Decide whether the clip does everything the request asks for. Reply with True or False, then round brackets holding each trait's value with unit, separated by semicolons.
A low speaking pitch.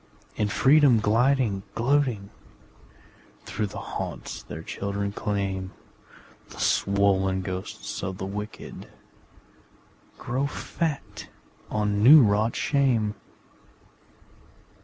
True (105 Hz)